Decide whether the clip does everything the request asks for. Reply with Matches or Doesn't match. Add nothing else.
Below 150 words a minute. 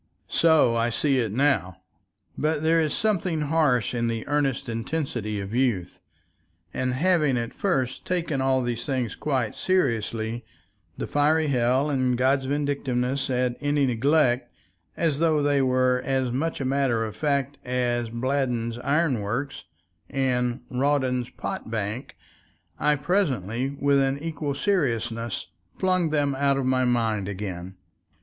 Matches